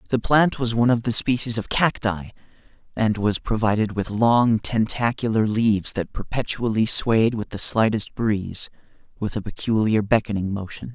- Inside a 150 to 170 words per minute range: Yes, average, 155 wpm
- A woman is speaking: No, male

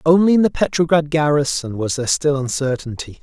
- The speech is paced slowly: No, average, 165 wpm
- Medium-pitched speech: Yes, medium, 145 Hz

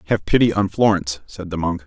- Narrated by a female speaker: No, male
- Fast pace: Yes, fast, 225 wpm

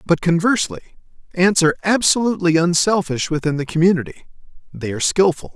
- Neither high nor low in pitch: Yes, medium, 175 Hz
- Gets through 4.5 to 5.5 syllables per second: No, 6.6 syllables/s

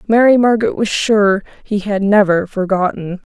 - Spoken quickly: No, average, 145 wpm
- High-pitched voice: Yes, high, 205 Hz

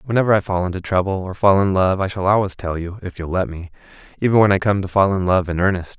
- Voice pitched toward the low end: Yes, very low, 95 Hz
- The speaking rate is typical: No, fast, 270 wpm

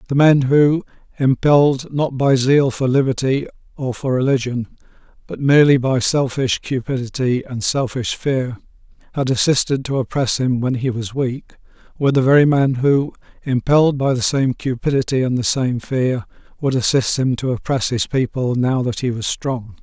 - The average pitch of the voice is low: Yes, low, 130 Hz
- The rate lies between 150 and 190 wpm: Yes, average, 165 wpm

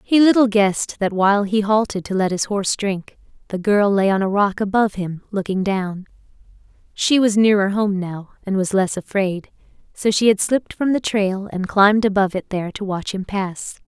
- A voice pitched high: Yes, high, 200 Hz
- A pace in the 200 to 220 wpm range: Yes, fast, 205 wpm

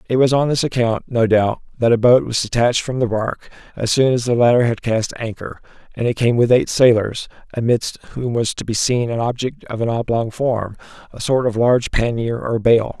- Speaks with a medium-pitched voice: No, low, 120 Hz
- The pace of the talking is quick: Yes, fast, 215 wpm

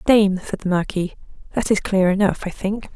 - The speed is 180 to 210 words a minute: Yes, fast, 205 wpm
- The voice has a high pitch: Yes, high, 195 Hz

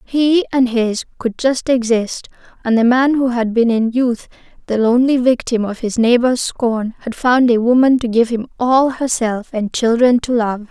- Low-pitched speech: No, high, 240 Hz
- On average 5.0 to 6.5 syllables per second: No, 4.5 syllables/s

